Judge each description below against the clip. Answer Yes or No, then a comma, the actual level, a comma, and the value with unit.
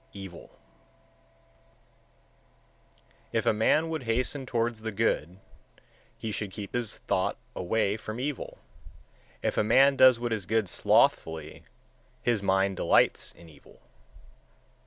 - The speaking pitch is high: No, low, 110 Hz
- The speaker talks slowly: Yes, slow, 125 wpm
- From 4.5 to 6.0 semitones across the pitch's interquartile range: No, average, 3.8 semitones